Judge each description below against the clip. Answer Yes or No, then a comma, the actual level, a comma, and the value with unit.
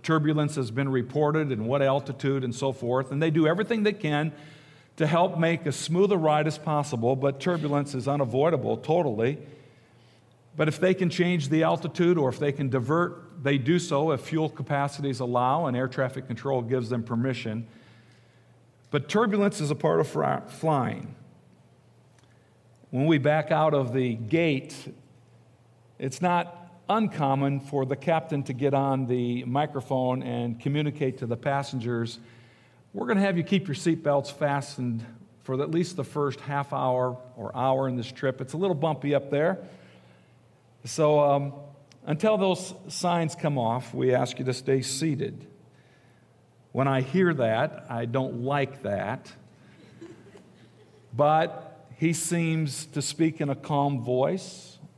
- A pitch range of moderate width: Yes, average, 3.8 semitones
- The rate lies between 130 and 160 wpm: Yes, average, 155 wpm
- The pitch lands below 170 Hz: Yes, medium, 140 Hz